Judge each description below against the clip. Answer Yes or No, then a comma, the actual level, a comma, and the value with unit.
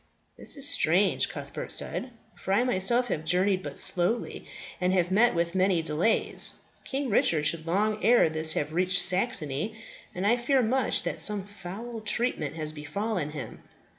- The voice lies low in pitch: No, medium, 185 Hz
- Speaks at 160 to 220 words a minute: Yes, average, 165 wpm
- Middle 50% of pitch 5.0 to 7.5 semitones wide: Yes, wide, 5.5 semitones